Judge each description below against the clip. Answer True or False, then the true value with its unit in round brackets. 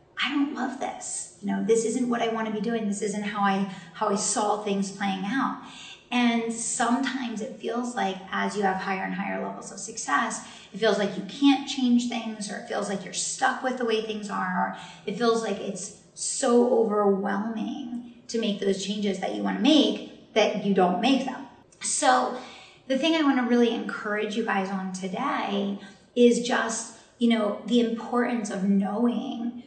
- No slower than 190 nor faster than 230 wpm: True (195 wpm)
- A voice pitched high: True (225 Hz)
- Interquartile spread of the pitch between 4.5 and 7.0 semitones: False (3.3 semitones)